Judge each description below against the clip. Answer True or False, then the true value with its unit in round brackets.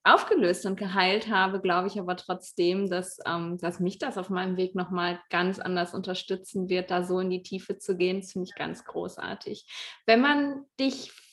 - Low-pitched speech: False (185 Hz)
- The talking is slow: False (185 wpm)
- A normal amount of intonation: False (1.9 semitones)